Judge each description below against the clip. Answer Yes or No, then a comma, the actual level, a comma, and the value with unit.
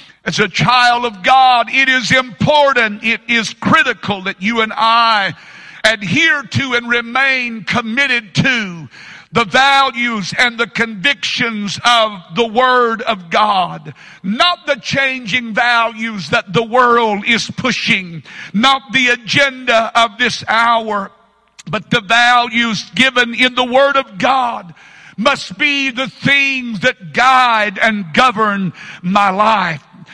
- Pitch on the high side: Yes, high, 230 Hz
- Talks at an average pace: No, slow, 130 wpm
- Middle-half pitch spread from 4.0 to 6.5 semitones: No, average, 3.5 semitones